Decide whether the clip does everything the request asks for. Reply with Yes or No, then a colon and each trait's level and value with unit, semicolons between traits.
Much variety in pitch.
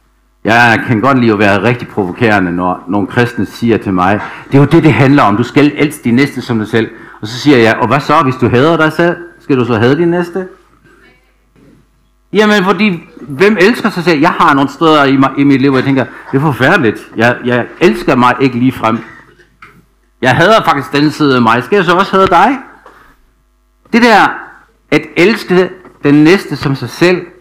Yes: wide, 5.8 semitones